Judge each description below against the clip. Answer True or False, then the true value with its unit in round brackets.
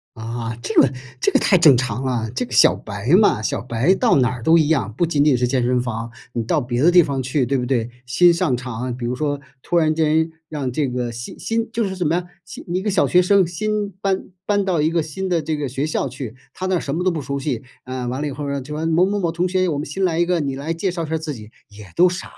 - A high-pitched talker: False (150 Hz)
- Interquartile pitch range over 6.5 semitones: False (5.7 semitones)